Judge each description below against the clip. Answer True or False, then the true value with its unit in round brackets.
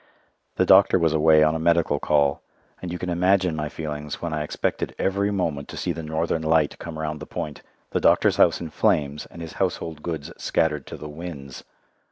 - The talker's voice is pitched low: True (80 Hz)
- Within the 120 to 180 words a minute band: False (205 wpm)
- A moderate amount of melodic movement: False (2.1 semitones)